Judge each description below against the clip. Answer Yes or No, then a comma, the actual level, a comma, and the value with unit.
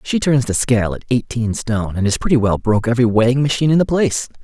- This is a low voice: Yes, low, 120 Hz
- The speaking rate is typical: No, fast, 245 wpm